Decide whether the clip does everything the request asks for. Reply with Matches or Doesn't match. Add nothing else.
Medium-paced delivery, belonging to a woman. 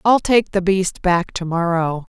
Matches